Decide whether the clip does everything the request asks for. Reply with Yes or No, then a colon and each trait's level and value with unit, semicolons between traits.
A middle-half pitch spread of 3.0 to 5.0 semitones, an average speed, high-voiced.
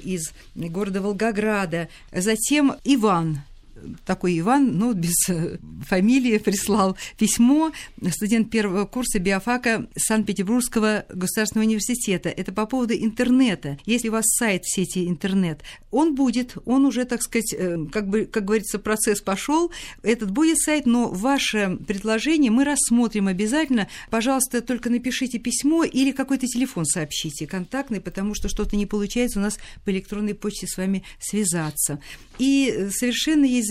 Yes: average, 4.3 semitones; average, 135 wpm; high, 215 Hz